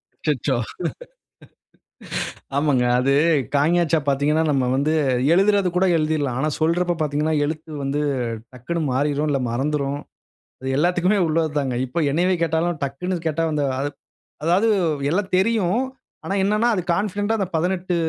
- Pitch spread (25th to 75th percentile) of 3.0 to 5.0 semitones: Yes, average, 4.0 semitones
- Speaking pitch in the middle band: Yes, medium, 160 Hz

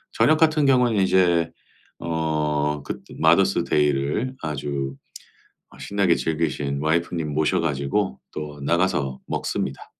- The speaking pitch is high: No, very low, 80 Hz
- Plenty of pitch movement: No, average, 4.4 semitones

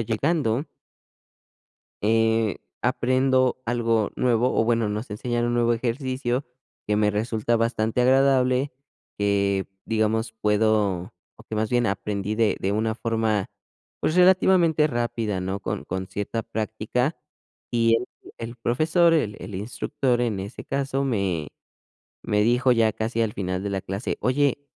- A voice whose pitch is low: Yes, low, 115 Hz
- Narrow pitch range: No, average, 3.2 semitones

